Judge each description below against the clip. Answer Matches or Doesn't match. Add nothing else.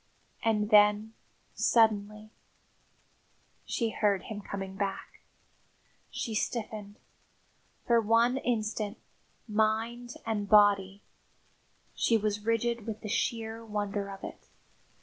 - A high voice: Matches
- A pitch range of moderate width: Doesn't match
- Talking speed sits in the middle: Doesn't match